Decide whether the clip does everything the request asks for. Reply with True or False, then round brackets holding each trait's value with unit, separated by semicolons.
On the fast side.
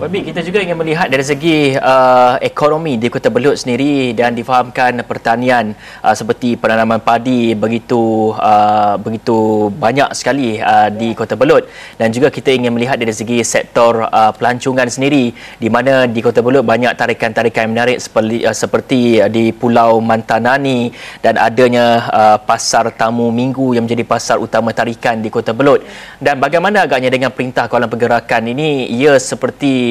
True (160 wpm)